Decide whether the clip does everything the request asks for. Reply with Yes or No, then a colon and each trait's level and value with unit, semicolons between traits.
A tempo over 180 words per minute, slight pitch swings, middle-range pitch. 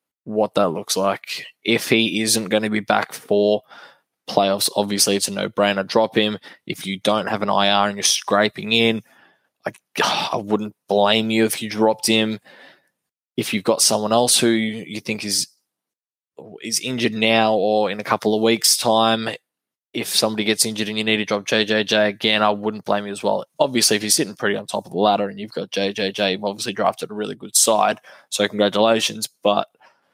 No: average, 195 wpm; narrow, 1.4 semitones; low, 110 Hz